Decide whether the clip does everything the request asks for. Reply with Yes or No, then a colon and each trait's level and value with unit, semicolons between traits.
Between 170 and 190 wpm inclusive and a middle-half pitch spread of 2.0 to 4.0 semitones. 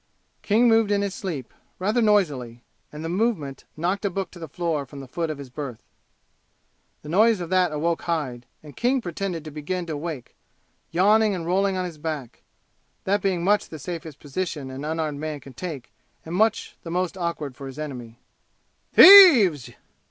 No: average, 180 wpm; average, 4.8 semitones